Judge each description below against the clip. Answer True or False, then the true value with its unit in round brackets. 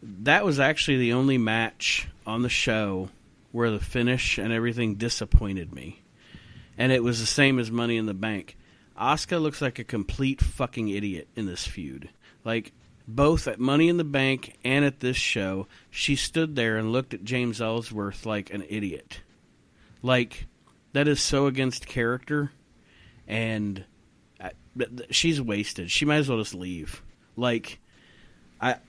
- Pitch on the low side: True (115 Hz)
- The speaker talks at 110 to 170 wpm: True (160 wpm)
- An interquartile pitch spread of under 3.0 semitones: False (4.0 semitones)